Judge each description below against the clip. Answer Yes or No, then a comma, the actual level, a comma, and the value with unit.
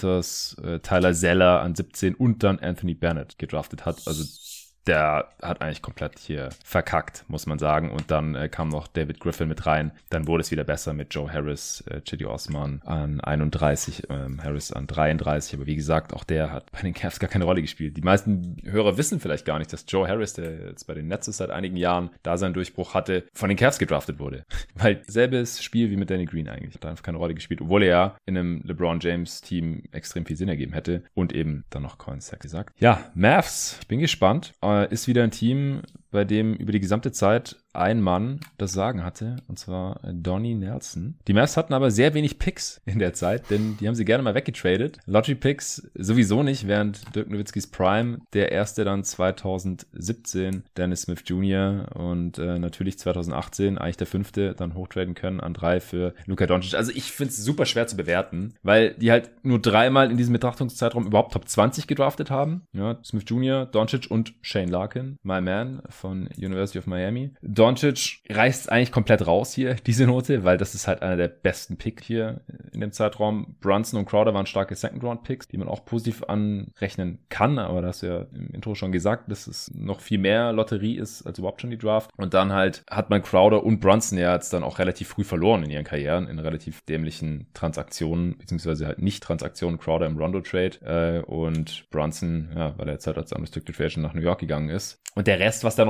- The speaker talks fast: Yes, fast, 200 wpm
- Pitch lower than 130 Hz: Yes, very low, 95 Hz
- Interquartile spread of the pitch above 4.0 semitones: Yes, average, 4.8 semitones